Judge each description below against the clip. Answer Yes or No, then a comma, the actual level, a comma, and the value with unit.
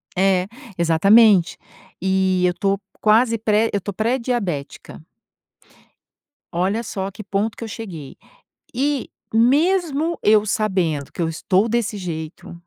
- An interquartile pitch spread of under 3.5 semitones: No, average, 4.0 semitones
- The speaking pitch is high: Yes, high, 205 Hz